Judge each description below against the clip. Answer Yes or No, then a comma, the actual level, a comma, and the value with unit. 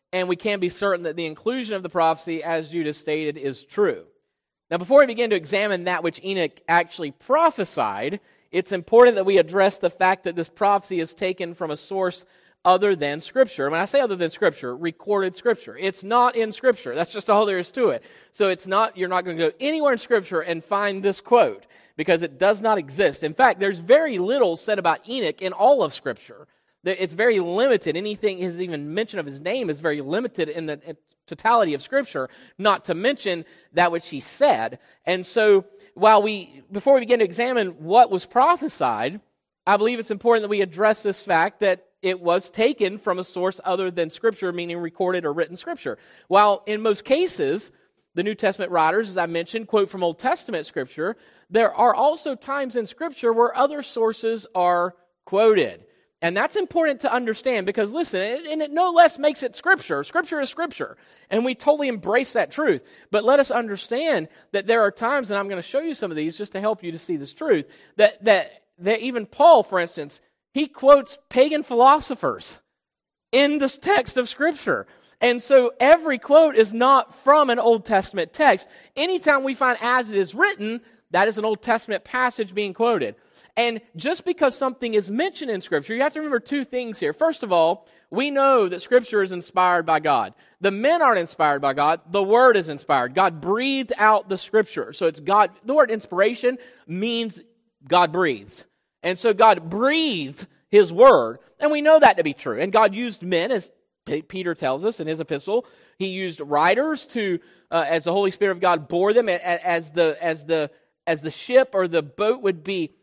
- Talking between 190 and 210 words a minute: Yes, average, 200 wpm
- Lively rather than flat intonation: Yes, wide, 6.0 semitones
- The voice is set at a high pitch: Yes, high, 205 Hz